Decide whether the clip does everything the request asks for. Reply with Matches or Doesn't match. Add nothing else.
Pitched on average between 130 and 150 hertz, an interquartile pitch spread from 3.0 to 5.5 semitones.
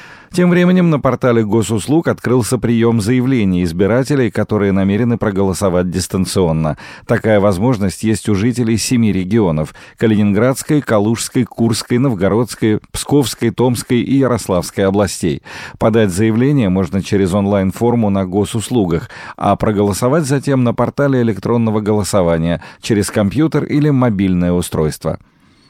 Doesn't match